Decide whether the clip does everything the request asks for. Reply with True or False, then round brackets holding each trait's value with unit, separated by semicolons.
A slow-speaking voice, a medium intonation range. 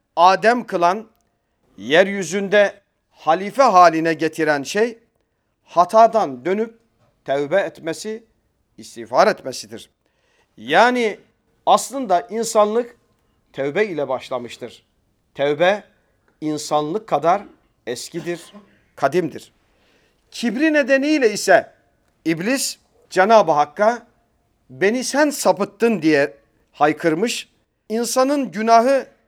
False (75 wpm; 7.5 semitones)